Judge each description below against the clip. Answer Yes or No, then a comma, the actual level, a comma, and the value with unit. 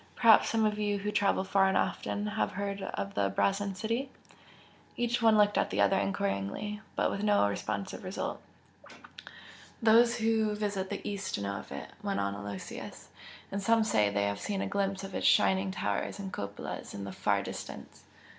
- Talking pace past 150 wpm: Yes, average, 185 wpm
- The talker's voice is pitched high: Yes, high, 195 Hz